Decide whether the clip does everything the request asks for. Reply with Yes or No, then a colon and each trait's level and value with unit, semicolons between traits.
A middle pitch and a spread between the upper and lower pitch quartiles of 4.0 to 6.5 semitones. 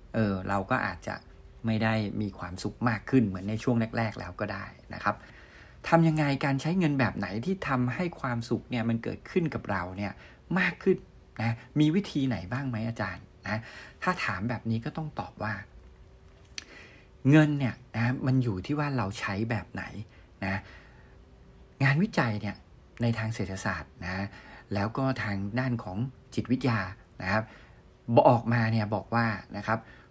No: low, 115 Hz; average, 4.3 semitones